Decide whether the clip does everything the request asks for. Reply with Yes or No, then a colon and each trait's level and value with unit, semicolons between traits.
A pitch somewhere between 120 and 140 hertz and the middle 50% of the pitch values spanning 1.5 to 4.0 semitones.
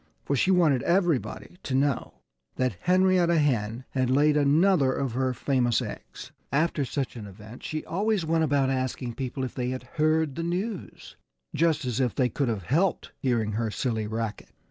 No: low, 135 Hz; average, 4.6 semitones